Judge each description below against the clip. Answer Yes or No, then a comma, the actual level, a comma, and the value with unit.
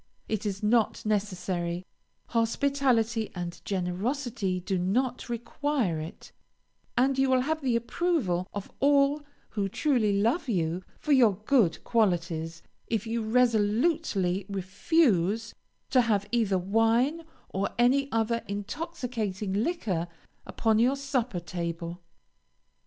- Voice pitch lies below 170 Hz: No, high, 220 Hz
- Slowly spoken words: Yes, slow, 115 wpm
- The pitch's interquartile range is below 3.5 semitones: No, average, 5.3 semitones